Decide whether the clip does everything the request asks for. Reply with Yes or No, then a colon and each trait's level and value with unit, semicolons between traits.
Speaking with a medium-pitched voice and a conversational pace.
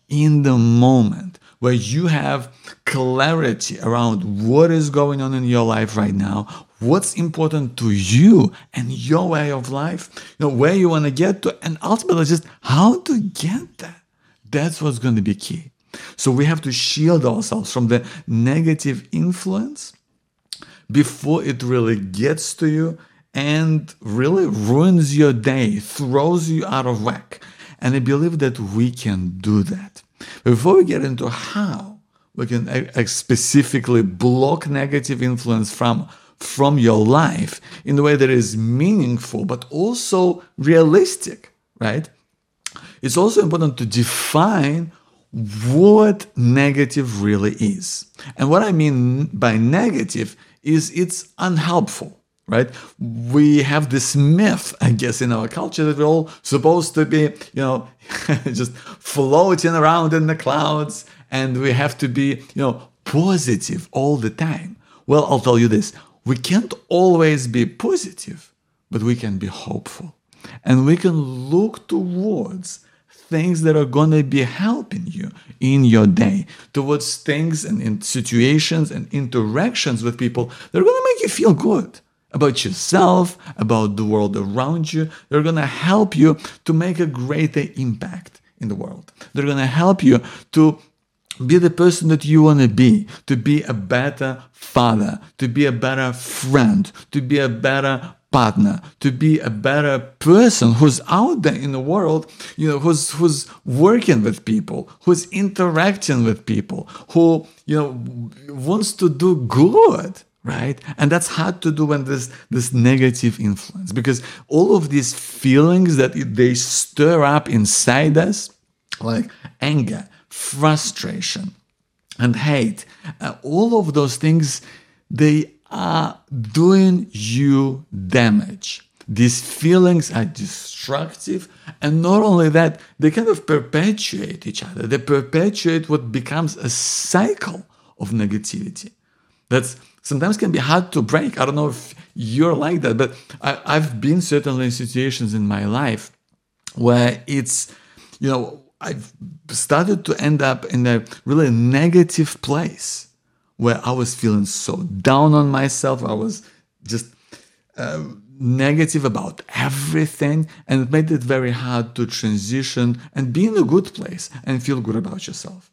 Yes: medium, 145 Hz; average, 150 wpm